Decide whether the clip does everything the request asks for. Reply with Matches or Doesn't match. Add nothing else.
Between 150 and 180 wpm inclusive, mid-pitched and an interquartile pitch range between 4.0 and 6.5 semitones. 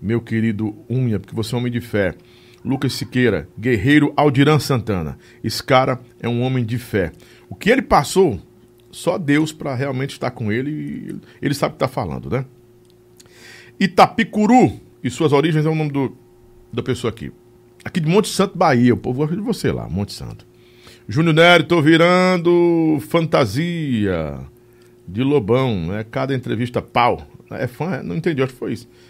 Doesn't match